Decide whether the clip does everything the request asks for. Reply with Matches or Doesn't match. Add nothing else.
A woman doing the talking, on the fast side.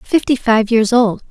Doesn't match